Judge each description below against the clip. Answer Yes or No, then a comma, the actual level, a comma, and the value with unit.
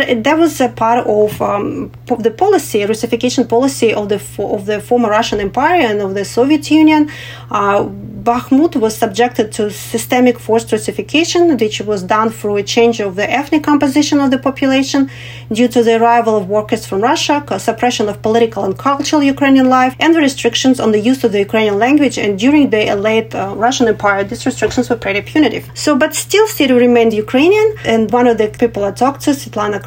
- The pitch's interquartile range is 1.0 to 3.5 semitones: No, average, 4.1 semitones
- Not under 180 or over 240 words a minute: Yes, average, 195 wpm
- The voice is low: No, high, 235 Hz